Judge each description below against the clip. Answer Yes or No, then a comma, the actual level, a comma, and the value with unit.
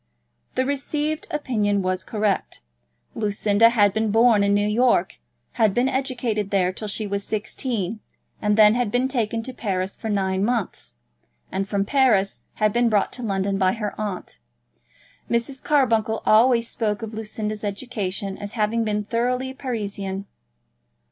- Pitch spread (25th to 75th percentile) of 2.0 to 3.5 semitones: Yes, average, 3.1 semitones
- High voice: Yes, high, 215 Hz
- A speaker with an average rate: Yes, average, 150 wpm